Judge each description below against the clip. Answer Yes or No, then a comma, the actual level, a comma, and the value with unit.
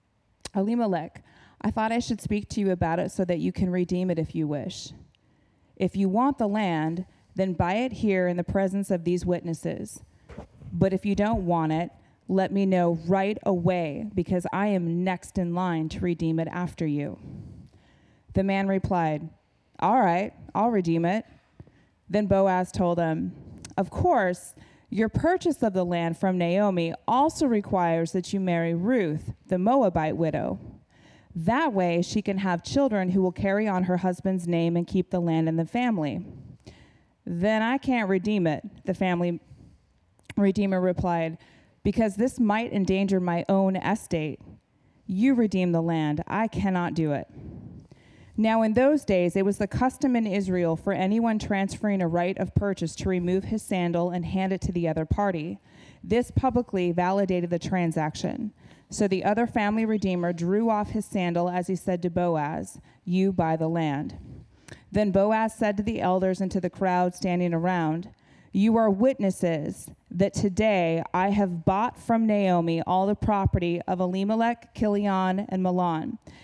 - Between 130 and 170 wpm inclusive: Yes, average, 165 wpm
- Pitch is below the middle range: No, medium, 185 Hz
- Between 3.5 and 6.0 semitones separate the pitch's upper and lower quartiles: No, average, 3.1 semitones